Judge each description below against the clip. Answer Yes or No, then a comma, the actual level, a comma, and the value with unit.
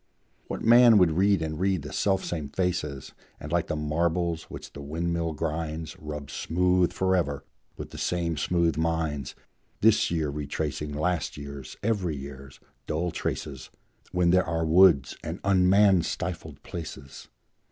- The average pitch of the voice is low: Yes, very low, 80 Hz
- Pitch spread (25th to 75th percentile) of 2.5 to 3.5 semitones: Yes, average, 3.2 semitones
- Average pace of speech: Yes, average, 145 wpm